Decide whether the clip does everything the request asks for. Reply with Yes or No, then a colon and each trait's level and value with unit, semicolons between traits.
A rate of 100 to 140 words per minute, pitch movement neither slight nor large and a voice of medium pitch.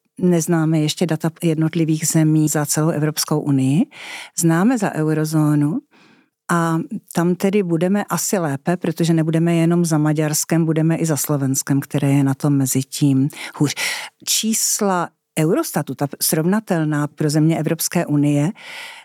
No: average, 130 wpm; narrow, 2.3 semitones; medium, 160 Hz